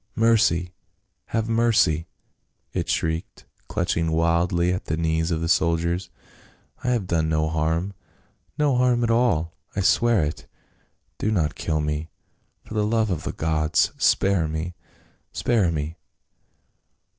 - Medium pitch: No, very low, 85 Hz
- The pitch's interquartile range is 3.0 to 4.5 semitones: No, average, 5.1 semitones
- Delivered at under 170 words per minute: Yes, average, 155 wpm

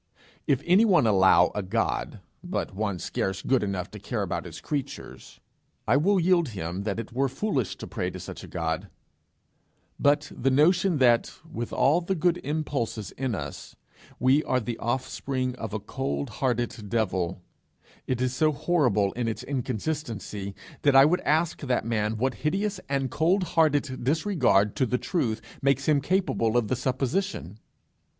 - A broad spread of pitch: Yes, wide, 5.8 semitones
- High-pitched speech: No, low, 130 Hz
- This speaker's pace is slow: No, average, 165 wpm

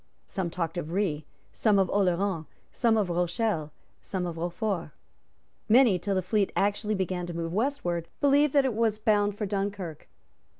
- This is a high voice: Yes, high, 195 Hz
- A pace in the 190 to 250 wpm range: No, average, 165 wpm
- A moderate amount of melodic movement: Yes, average, 3.7 semitones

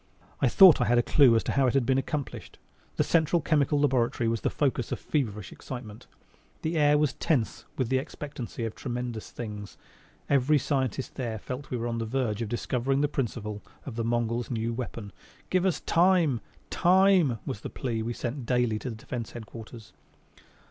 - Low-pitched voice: Yes, low, 125 Hz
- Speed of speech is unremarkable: Yes, average, 190 wpm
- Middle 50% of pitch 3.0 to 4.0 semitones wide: Yes, average, 3.7 semitones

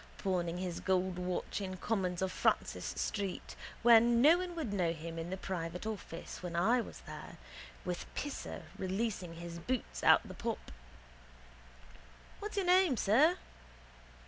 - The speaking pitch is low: No, high, 190 Hz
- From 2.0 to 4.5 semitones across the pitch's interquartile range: No, average, 5.1 semitones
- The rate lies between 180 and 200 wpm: No, average, 150 wpm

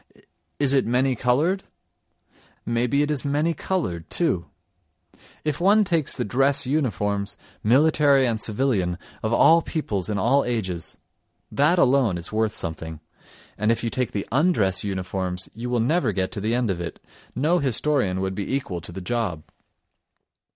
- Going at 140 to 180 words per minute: Yes, average, 160 wpm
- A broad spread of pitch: Yes, wide, 6.4 semitones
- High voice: No, low, 120 Hz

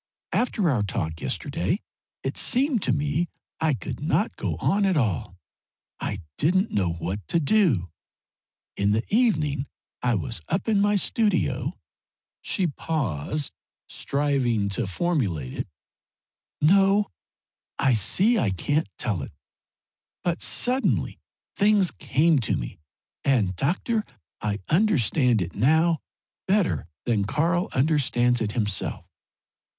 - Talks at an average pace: No, slow, 125 wpm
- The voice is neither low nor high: Yes, medium, 145 Hz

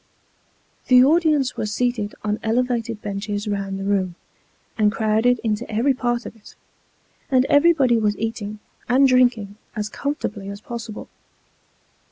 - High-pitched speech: Yes, high, 225 Hz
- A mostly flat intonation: No, average, 3.2 semitones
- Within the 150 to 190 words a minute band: No, average, 140 wpm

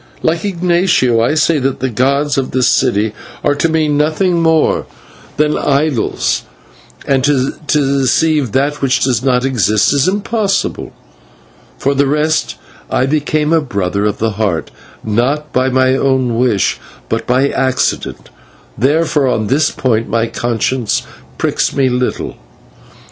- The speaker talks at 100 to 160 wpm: Yes, average, 140 wpm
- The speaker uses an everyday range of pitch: Yes, average, 3.5 semitones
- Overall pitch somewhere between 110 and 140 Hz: Yes, low, 135 Hz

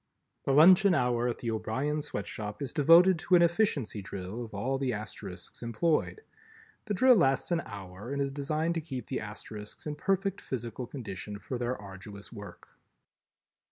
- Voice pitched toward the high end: No, low, 130 Hz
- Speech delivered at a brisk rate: No, average, 165 wpm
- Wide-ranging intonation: Yes, wide, 7.1 semitones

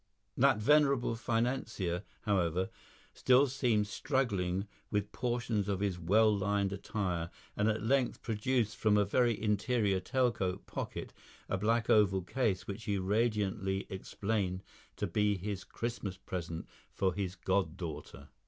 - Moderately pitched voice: No, low, 105 Hz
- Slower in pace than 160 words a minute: Yes, slow, 135 wpm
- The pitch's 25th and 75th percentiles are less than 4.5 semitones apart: Yes, average, 3.5 semitones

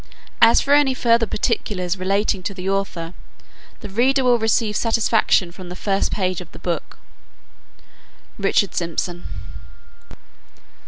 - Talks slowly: Yes, slow, 125 wpm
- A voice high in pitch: Yes, high, 200 Hz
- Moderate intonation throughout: Yes, average, 4.0 semitones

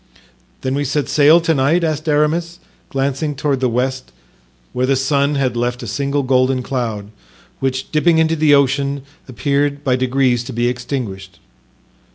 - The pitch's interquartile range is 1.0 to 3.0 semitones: Yes, narrow, 2.4 semitones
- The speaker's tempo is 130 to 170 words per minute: Yes, average, 160 wpm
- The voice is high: No, low, 135 Hz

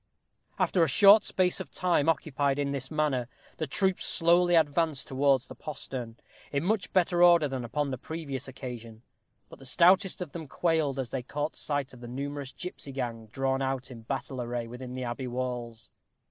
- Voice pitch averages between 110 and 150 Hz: Yes, medium, 140 Hz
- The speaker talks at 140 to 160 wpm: No, average, 185 wpm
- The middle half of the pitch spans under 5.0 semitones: Yes, average, 4.4 semitones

